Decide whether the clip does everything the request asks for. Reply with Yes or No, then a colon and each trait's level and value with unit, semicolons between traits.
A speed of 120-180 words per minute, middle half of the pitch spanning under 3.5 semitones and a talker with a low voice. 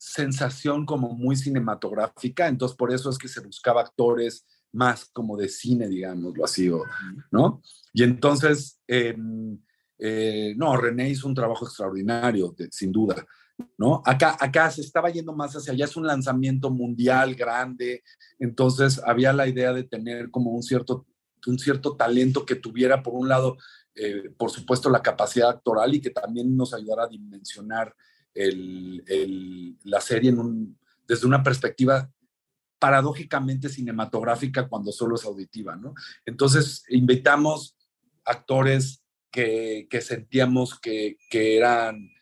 Yes: average, 145 wpm; average, 3.1 semitones; low, 125 Hz